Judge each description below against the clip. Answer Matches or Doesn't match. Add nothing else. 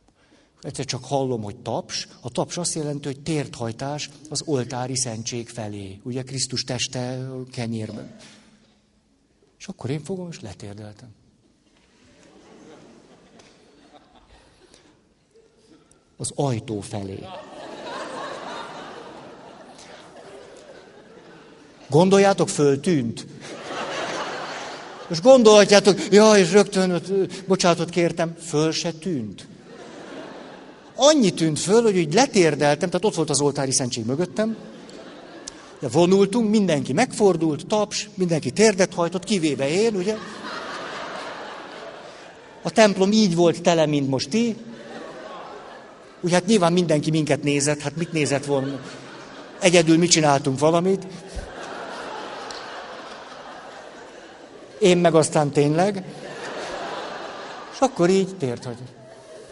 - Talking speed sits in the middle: Doesn't match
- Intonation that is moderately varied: Doesn't match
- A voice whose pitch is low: Doesn't match